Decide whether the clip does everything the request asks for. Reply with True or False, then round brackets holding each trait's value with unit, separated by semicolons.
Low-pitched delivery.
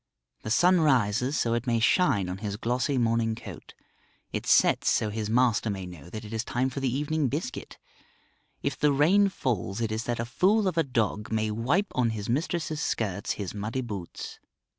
True (120 Hz)